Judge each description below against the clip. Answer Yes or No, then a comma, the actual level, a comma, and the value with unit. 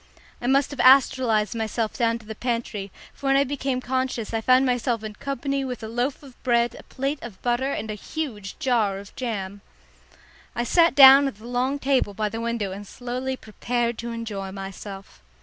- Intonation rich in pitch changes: No, average, 3.4 semitones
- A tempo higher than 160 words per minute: Yes, average, 195 wpm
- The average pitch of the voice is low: No, high, 240 Hz